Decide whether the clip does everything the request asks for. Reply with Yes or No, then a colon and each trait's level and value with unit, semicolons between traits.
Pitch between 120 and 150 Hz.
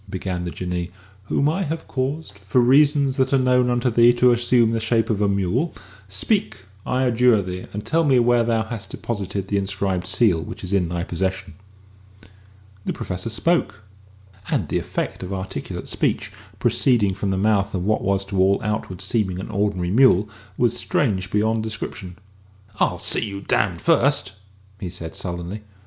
No: low, 105 Hz